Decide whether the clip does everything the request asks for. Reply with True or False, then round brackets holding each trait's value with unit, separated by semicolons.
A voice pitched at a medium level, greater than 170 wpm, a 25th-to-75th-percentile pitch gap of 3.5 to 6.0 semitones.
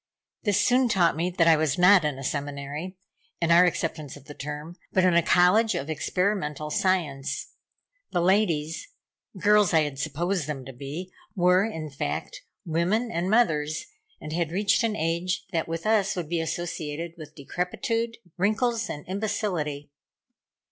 False (170 Hz; 160 wpm; 4.3 semitones)